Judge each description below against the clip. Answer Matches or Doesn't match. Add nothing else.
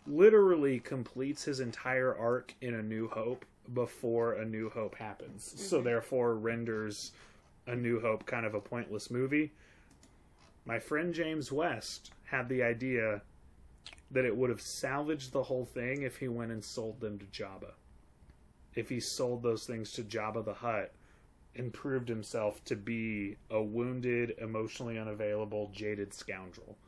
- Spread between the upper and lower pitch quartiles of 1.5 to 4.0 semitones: Matches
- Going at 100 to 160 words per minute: Matches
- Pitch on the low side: Matches